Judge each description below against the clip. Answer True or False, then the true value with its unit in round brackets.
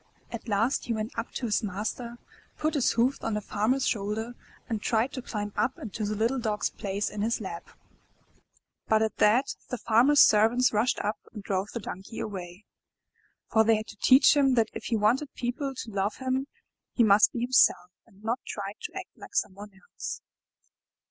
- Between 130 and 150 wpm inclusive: False (195 wpm)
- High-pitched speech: True (220 Hz)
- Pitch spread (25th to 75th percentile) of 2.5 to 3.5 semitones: True (2.9 semitones)